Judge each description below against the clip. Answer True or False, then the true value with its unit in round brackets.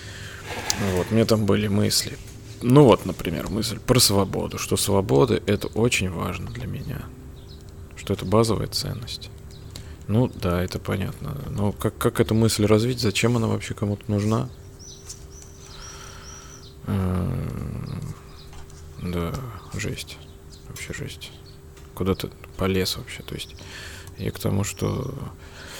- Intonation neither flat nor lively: True (4.5 semitones)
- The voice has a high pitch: False (100 Hz)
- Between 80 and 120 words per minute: True (115 wpm)